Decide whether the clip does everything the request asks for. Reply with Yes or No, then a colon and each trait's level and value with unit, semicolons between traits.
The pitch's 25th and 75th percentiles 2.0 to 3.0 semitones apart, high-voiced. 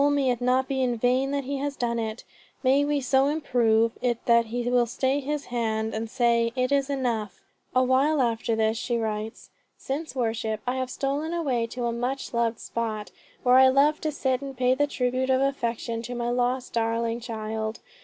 Yes: average, 2.7 semitones; high, 245 Hz